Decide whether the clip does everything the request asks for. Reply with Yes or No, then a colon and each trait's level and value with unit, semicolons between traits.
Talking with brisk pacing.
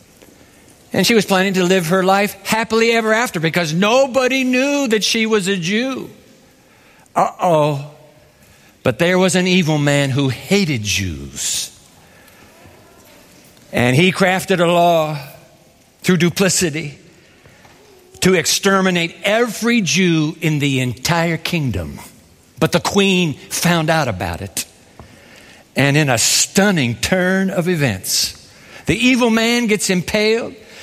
No: slow, 125 wpm